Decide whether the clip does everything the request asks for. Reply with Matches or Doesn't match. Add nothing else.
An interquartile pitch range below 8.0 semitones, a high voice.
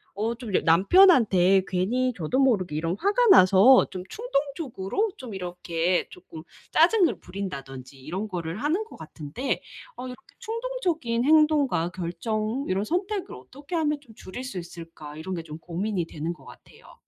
Doesn't match